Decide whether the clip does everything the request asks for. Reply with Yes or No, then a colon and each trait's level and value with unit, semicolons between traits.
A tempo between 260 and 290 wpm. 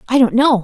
Yes: fast, 285 wpm